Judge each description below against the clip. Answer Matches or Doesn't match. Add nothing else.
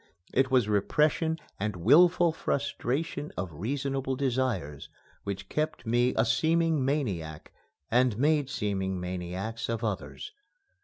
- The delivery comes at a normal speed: Doesn't match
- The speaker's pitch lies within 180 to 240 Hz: Doesn't match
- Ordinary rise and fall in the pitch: Doesn't match